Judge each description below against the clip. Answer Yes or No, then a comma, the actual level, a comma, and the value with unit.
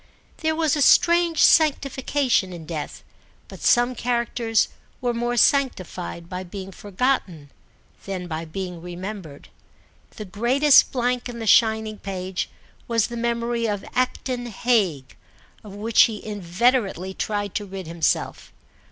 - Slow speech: Yes, slow, 130 wpm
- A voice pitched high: Yes, high, 220 Hz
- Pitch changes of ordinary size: Yes, average, 4.7 semitones